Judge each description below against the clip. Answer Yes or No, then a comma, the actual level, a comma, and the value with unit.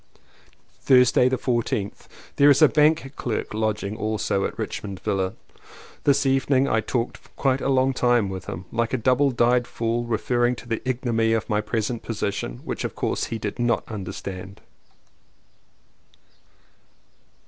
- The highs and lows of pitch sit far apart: No, average, 3.3 semitones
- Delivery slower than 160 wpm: Yes, average, 150 wpm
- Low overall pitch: Yes, low, 120 Hz